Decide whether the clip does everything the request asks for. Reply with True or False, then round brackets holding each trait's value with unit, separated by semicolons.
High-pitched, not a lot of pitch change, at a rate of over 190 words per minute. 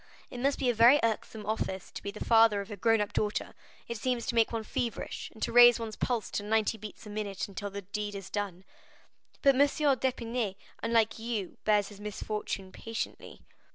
True (220 Hz; 2.3 semitones; 200 wpm)